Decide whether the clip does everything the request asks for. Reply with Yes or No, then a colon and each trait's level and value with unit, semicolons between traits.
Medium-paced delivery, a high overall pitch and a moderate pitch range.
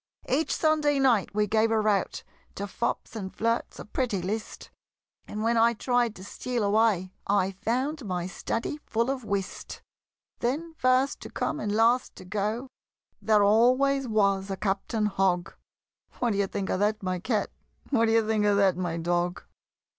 Yes: average, 170 wpm; high, 215 Hz; average, 3.7 semitones